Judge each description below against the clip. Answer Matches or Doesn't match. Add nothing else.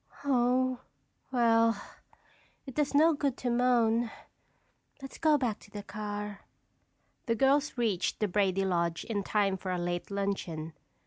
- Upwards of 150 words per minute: Doesn't match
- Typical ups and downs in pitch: Matches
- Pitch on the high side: Matches